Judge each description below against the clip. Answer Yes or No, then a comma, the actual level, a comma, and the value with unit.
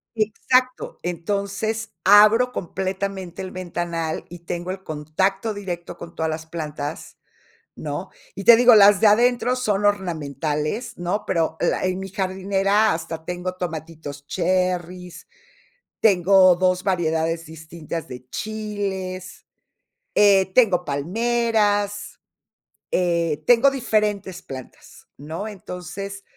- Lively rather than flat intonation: No, average, 3.6 semitones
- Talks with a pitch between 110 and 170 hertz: No, medium, 185 Hz